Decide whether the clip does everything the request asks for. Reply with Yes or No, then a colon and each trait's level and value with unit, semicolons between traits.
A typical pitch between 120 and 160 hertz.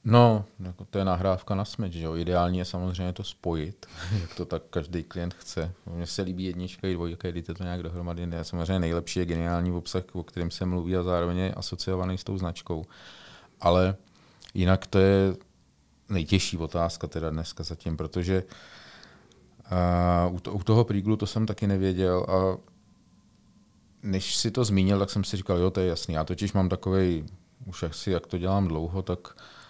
No: very low, 90 Hz